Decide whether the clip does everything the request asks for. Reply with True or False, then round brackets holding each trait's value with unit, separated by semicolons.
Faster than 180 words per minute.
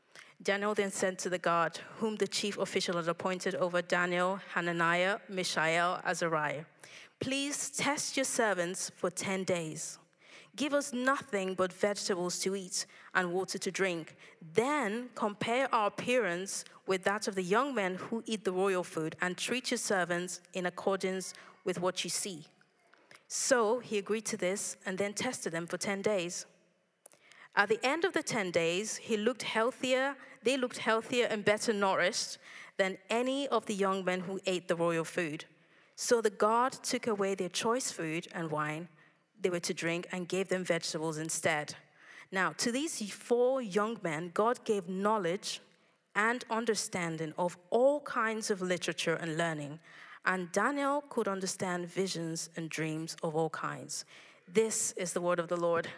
False (165 wpm)